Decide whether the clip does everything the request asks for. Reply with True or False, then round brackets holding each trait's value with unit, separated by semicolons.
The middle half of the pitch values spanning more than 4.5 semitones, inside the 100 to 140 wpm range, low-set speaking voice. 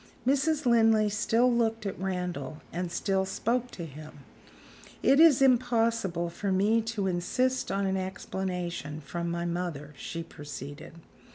False (5.2 semitones; 135 wpm; 190 Hz)